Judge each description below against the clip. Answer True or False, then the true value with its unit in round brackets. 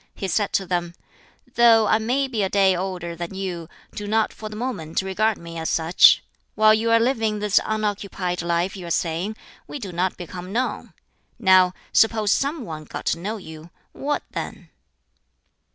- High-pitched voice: True (195 Hz)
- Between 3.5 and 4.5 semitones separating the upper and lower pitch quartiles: True (3.9 semitones)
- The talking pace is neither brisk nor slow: True (180 wpm)